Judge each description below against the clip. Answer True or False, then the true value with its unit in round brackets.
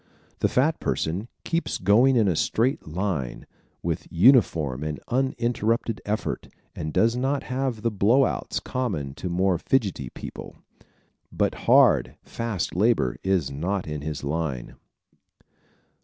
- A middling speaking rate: False (130 wpm)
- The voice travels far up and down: True (7.5 semitones)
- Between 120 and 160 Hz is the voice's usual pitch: False (100 Hz)